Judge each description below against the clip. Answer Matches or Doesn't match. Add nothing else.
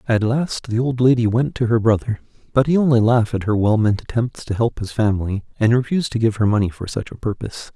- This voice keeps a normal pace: Doesn't match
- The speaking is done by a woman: Doesn't match